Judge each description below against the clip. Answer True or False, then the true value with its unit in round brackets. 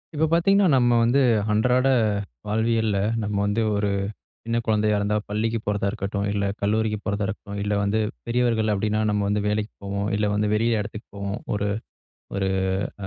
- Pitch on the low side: True (105 Hz)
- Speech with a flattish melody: True (2.0 semitones)